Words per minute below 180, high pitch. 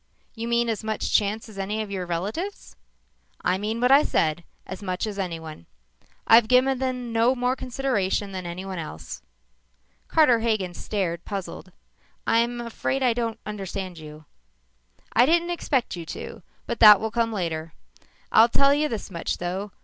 Yes: average, 165 wpm; high, 215 Hz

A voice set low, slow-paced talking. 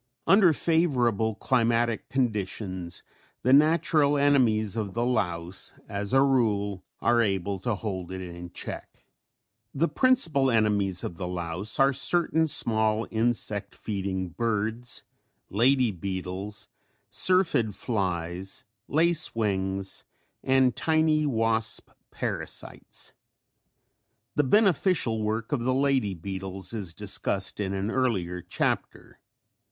Yes: low, 110 Hz; slow, 110 wpm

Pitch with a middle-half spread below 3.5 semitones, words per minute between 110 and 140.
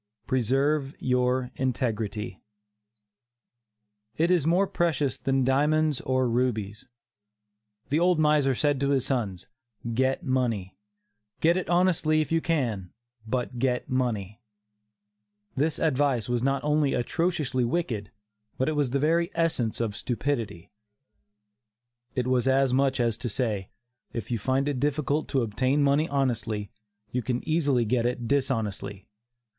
No: average, 3.8 semitones; slow, 135 wpm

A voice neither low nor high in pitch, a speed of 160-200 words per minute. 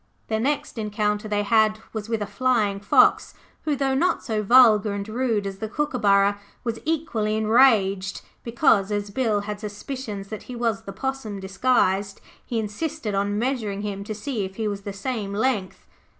No: high, 215 Hz; average, 175 wpm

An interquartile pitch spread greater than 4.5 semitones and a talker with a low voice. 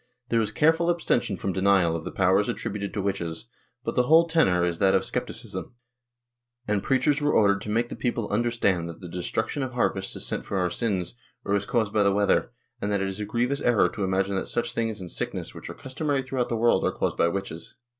No: average, 4.0 semitones; low, 105 Hz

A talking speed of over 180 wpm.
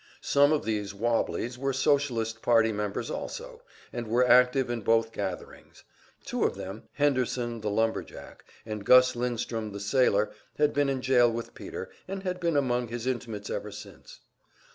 No: average, 165 wpm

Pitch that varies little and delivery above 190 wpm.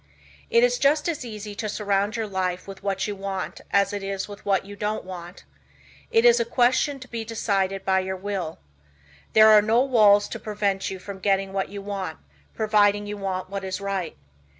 Yes: narrow, 2.1 semitones; average, 200 wpm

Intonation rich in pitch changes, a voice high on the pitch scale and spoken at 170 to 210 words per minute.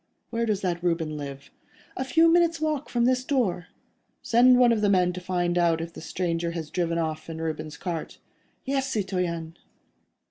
No: wide, 6.6 semitones; medium, 180 Hz; average, 180 wpm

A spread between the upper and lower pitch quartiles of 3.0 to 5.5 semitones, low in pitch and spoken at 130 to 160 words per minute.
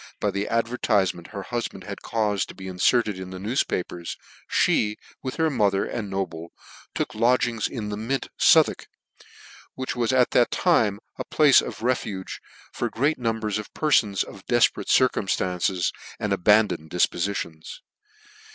Yes: average, 4.1 semitones; low, 105 Hz; average, 150 wpm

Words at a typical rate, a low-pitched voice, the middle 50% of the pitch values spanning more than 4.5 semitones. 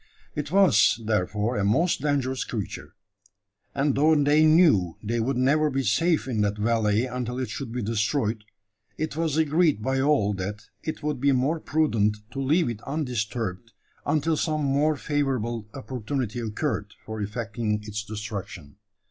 Yes: average, 155 wpm; low, 125 Hz; wide, 5.6 semitones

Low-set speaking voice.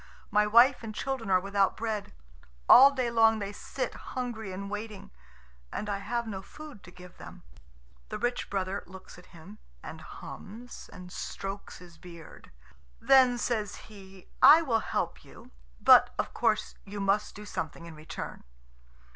No: high, 205 Hz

